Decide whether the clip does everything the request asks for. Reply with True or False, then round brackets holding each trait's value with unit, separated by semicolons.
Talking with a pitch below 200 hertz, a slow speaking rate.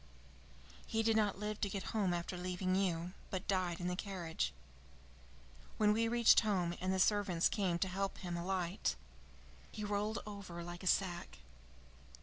False (190 Hz; 160 wpm)